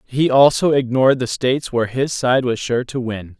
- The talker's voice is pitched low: Yes, low, 125 Hz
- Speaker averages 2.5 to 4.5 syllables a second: No, 5.2 syllables/s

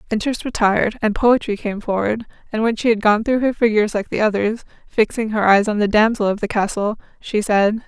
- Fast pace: Yes, fast, 215 wpm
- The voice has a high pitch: Yes, high, 215 Hz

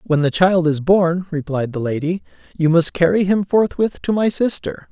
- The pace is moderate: Yes, average, 195 wpm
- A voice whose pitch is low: No, medium, 175 Hz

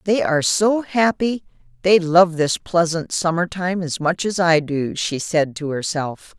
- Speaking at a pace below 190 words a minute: Yes, average, 180 wpm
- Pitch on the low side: No, medium, 170 Hz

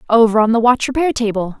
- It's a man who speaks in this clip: No, female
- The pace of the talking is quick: Yes, fast, 225 wpm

